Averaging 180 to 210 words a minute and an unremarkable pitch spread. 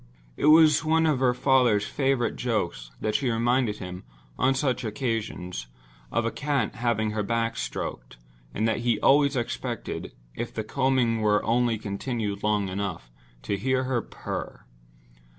No: average, 150 wpm; average, 4.0 semitones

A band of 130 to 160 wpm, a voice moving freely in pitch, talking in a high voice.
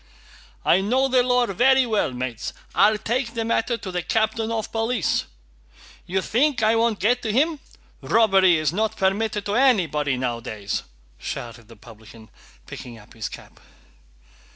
Yes: average, 155 wpm; wide, 8.5 semitones; high, 210 Hz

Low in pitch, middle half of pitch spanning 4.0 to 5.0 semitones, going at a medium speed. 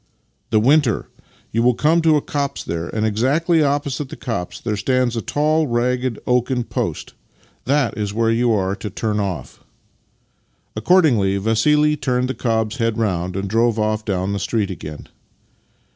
Yes: low, 115 Hz; average, 4.6 semitones; average, 170 wpm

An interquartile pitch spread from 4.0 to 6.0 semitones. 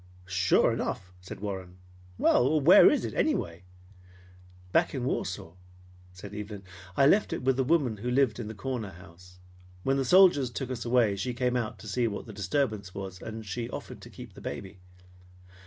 Yes: average, 5.1 semitones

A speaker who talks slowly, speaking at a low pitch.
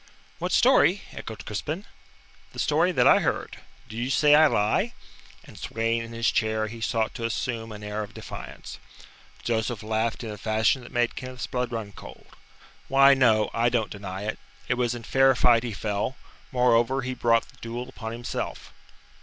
No: average, 180 wpm; low, 115 Hz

